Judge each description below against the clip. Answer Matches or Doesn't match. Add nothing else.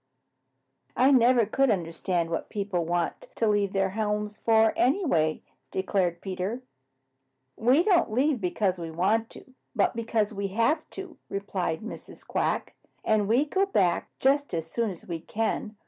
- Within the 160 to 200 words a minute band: Doesn't match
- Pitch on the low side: Doesn't match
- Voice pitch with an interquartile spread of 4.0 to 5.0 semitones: Matches